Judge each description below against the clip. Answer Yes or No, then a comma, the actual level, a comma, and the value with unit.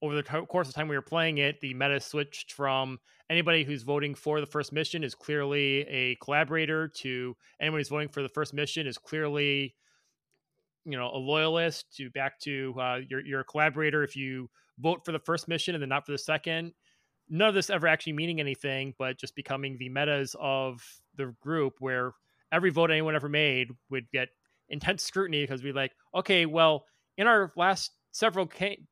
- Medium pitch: Yes, medium, 145 Hz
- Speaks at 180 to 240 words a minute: Yes, average, 200 wpm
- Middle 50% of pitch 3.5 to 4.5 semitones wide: No, average, 3.0 semitones